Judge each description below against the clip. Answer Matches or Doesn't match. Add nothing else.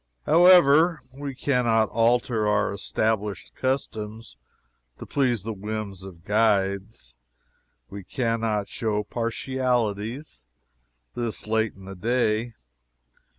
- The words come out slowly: Matches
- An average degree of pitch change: Matches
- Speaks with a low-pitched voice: Matches